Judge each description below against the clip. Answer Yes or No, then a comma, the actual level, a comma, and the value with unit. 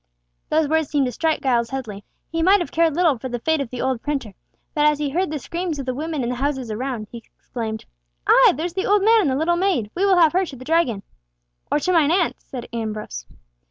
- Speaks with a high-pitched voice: Yes, very high, 290 Hz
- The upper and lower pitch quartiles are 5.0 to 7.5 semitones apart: Yes, average, 5.3 semitones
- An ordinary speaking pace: No, fast, 245 wpm